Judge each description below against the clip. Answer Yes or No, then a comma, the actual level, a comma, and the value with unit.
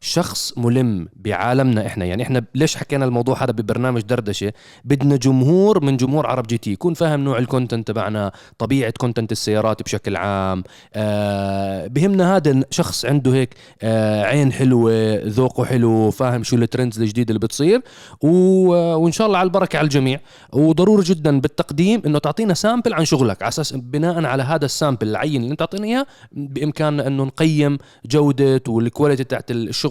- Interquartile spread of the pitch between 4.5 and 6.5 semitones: Yes, average, 4.8 semitones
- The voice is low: Yes, low, 130 Hz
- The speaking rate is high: Yes, fast, 155 wpm